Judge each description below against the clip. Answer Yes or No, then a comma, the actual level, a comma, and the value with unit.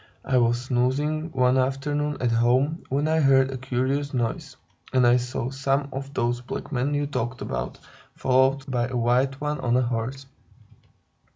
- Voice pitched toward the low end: Yes, low, 130 Hz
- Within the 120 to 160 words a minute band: No, average, 170 wpm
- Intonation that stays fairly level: Yes, narrow, 2.3 semitones